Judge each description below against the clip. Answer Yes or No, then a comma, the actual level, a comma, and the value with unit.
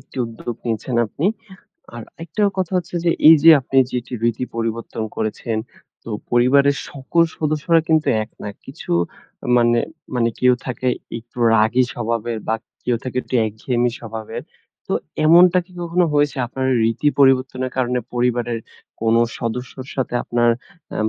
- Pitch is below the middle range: Yes, low, 125 Hz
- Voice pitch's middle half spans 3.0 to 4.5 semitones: Yes, average, 3.4 semitones